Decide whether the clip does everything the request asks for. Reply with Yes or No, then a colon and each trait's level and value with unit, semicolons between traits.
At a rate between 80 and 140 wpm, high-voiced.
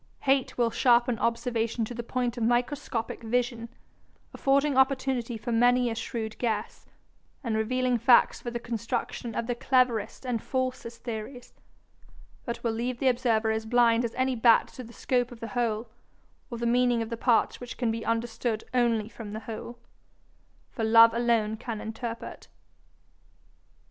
No: average, 160 wpm; high, 235 Hz